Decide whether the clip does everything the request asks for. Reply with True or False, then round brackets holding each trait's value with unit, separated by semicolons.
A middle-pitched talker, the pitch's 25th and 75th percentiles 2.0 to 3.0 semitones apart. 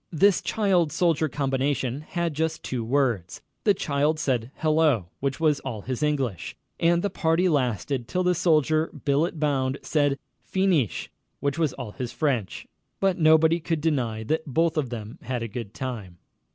False (145 Hz; 4.3 semitones)